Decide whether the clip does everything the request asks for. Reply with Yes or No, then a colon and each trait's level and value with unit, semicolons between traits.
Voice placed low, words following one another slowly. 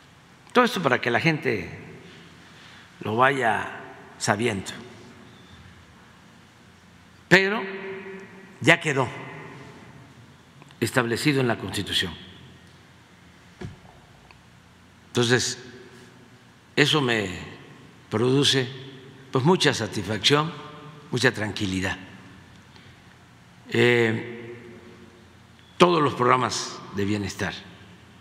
Yes: low, 125 Hz; slow, 65 wpm